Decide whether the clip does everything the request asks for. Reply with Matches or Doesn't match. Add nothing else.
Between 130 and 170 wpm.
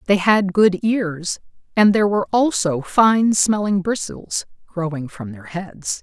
Matches